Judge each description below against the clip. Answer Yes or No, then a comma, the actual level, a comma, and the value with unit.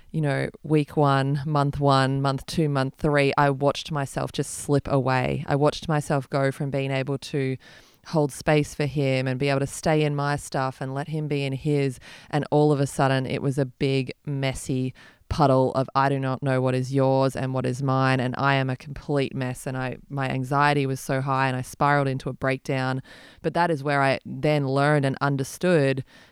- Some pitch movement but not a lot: No, narrow, 1.5 semitones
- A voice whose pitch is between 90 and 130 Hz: No, medium, 140 Hz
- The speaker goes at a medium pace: No, fast, 210 wpm